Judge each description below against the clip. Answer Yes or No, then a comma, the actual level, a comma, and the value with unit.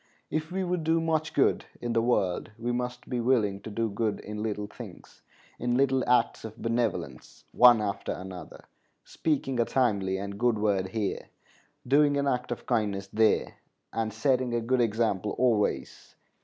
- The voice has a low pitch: Yes, low, 115 Hz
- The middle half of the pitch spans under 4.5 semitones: Yes, average, 3.5 semitones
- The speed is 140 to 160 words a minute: No, average, 170 wpm